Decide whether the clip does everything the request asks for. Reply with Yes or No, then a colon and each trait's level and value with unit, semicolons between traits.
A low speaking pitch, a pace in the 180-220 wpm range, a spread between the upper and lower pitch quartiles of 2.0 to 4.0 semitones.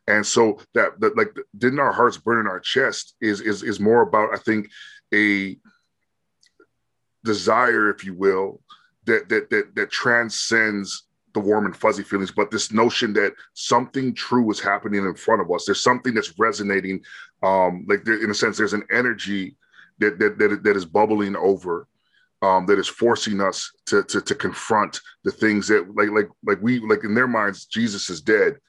Yes: low, 105 Hz; average, 185 wpm; average, 2.9 semitones